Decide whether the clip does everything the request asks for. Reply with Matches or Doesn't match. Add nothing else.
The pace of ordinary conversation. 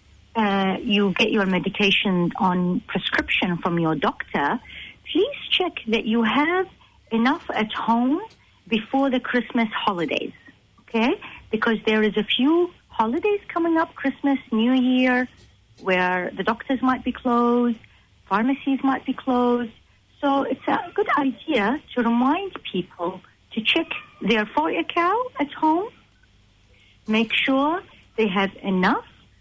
Doesn't match